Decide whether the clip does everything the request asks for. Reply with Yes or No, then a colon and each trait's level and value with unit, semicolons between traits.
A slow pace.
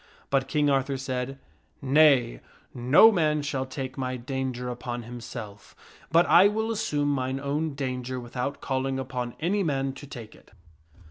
No: average, 155 wpm